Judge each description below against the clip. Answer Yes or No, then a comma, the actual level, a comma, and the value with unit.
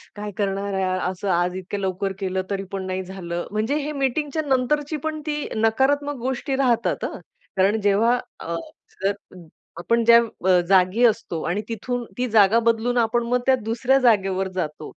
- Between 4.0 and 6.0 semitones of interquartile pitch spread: Yes, average, 4.7 semitones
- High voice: Yes, high, 215 Hz